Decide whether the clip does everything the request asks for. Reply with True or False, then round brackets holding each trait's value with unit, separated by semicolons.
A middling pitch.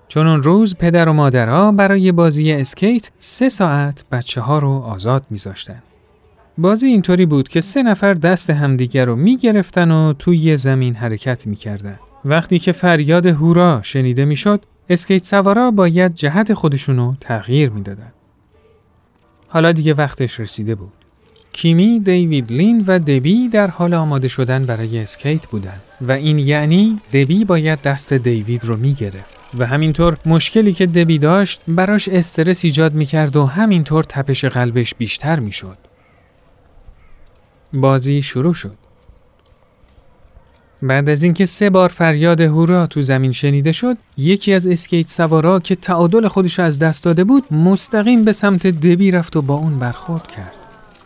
True (155 Hz)